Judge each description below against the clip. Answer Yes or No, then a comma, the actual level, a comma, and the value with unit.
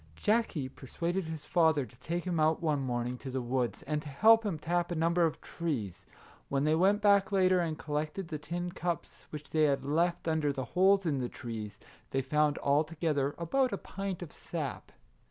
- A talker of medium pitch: Yes, medium, 160 Hz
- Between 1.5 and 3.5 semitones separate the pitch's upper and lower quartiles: No, average, 3.9 semitones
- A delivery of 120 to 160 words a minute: No, fast, 205 wpm